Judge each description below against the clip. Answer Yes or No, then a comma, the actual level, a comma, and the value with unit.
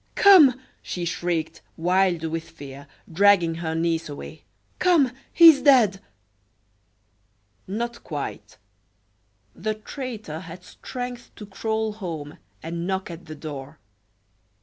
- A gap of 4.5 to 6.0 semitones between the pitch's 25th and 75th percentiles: Yes, wide, 5.5 semitones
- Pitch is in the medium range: Yes, medium, 180 Hz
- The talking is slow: Yes, slow, 115 wpm